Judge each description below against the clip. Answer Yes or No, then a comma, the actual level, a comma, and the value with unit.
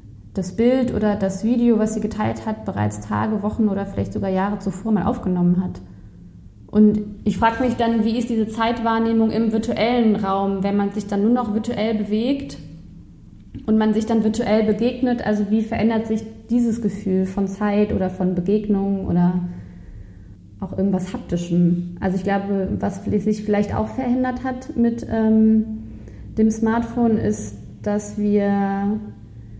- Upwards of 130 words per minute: Yes, average, 155 wpm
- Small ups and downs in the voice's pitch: No, average, 3.2 semitones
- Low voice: No, high, 210 Hz